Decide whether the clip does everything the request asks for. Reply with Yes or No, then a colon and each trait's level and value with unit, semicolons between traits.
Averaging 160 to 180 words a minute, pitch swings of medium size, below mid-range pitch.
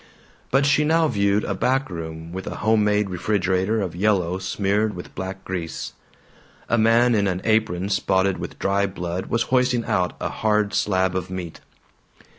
Yes: average, 165 wpm; average, 3.0 semitones; low, 100 Hz